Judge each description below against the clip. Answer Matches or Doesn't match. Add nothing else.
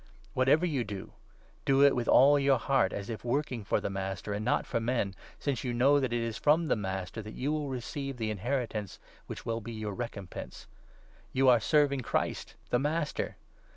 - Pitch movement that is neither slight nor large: Matches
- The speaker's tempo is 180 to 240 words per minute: Matches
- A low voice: Matches